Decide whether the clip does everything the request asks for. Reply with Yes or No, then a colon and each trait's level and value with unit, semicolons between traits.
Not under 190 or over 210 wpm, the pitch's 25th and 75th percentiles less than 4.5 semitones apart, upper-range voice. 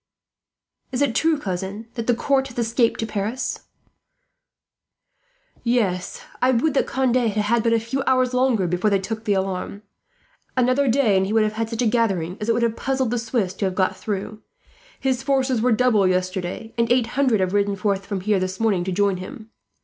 Yes: fast, 205 wpm; average, 4.1 semitones; high, 225 Hz